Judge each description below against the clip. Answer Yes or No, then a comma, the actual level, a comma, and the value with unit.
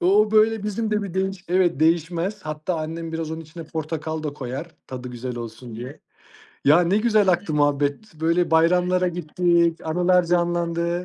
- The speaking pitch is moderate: Yes, medium, 170 Hz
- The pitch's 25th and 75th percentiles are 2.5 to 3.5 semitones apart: Yes, average, 2.8 semitones